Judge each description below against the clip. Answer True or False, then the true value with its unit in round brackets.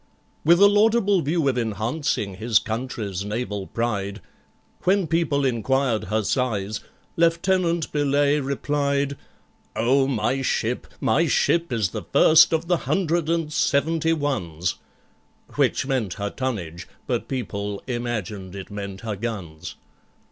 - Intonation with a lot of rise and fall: True (7.1 semitones)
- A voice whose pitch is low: True (130 Hz)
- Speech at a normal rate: False (125 wpm)